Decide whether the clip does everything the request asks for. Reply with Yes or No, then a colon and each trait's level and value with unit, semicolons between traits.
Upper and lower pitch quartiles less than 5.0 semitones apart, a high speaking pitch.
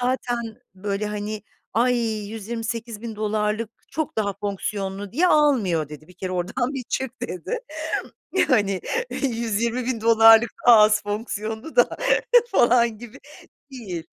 Yes: average, 2.8 semitones; high, 225 Hz